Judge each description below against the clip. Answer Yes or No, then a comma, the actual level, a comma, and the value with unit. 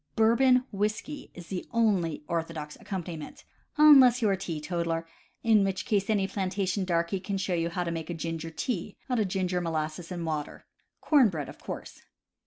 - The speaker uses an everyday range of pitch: Yes, average, 4.2 semitones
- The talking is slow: No, average, 180 wpm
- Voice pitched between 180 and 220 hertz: Yes, medium, 185 Hz